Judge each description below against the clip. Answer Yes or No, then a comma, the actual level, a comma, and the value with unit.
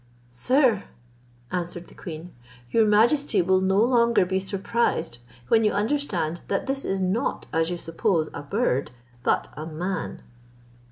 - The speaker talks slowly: No, average, 145 wpm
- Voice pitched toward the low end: No, high, 190 Hz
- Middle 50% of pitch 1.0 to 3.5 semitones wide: No, average, 5.2 semitones